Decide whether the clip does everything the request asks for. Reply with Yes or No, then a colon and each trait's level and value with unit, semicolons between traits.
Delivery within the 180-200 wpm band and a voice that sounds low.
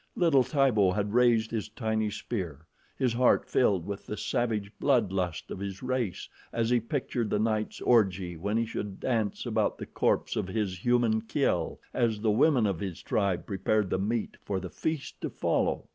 Yes: average, 185 wpm; low, 110 Hz